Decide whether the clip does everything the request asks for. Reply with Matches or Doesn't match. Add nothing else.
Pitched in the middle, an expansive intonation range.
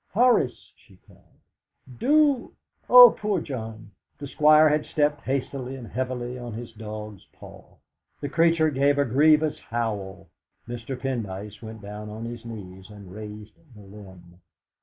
Doesn't match